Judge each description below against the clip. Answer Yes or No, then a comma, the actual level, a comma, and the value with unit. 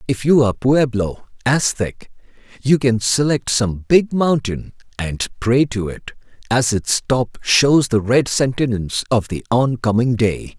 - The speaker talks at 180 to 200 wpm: No, average, 155 wpm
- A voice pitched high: No, low, 120 Hz